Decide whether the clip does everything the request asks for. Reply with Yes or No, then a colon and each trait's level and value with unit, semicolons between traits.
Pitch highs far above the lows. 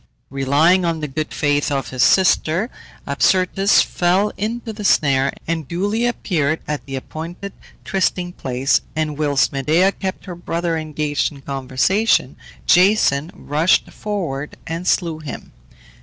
No: average, 4.7 semitones